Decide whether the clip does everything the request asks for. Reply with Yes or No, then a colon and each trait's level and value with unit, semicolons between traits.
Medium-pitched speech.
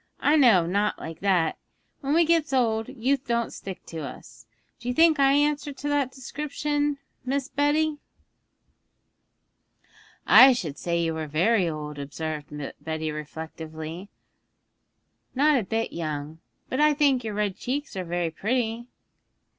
No: high, 225 Hz